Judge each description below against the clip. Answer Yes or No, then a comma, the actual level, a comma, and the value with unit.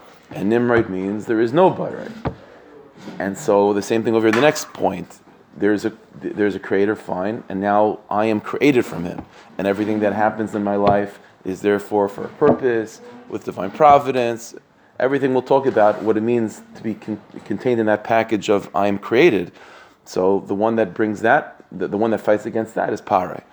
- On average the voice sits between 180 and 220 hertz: No, low, 105 Hz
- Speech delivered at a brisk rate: No, average, 195 wpm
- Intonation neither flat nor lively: No, narrow, 1.9 semitones